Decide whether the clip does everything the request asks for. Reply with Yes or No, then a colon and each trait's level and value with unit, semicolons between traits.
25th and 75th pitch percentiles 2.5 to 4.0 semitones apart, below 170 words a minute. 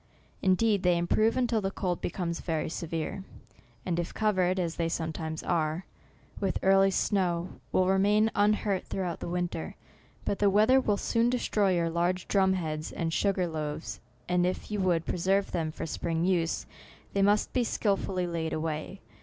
No: average, 3.1 semitones; average, 175 wpm